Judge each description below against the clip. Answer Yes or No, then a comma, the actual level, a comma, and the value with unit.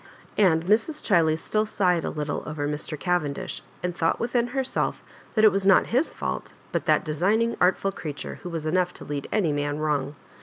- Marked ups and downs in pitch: Yes, wide, 5.7 semitones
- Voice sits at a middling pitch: Yes, medium, 175 Hz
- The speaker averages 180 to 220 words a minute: Yes, average, 190 wpm